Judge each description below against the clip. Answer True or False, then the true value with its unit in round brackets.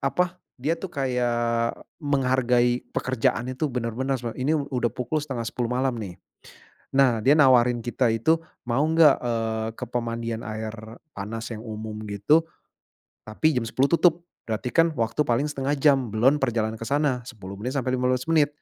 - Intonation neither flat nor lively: True (3.2 semitones)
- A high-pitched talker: False (125 Hz)